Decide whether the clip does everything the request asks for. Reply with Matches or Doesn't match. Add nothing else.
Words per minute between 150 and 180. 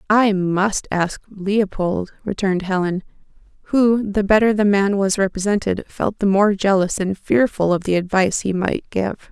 Matches